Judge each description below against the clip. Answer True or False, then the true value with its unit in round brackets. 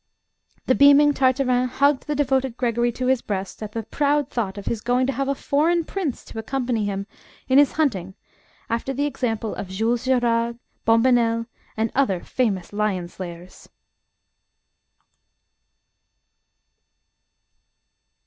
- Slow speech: True (130 wpm)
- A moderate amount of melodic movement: True (3.8 semitones)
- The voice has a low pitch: False (245 Hz)